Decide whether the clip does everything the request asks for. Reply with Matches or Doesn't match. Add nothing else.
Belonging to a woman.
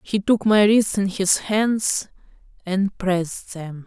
Matches